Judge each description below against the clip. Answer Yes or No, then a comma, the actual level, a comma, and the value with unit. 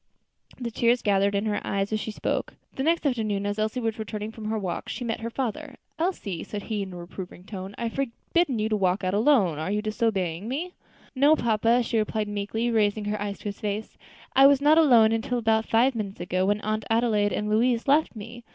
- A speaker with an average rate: No, fast, 225 wpm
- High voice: Yes, high, 220 Hz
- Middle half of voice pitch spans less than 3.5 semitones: Yes, average, 2.8 semitones